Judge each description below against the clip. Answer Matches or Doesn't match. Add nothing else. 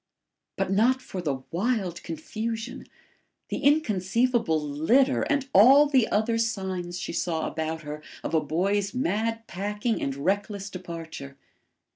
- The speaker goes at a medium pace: Doesn't match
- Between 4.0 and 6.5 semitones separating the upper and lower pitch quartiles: Matches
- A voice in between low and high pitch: Doesn't match